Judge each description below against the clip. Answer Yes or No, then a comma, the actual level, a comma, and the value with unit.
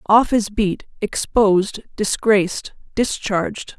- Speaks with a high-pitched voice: Yes, high, 205 Hz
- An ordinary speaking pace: No, slow, 95 wpm